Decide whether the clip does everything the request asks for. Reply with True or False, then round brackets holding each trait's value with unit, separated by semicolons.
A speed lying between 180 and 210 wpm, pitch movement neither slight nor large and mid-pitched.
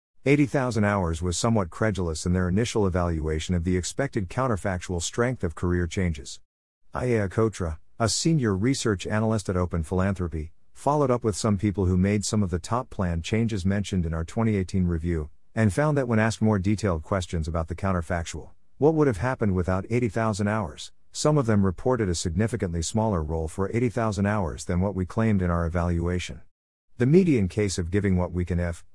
False (185 wpm; 4.2 semitones; 95 Hz)